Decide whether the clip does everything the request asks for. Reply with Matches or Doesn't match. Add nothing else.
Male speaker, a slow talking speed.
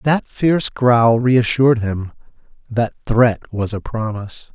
Matches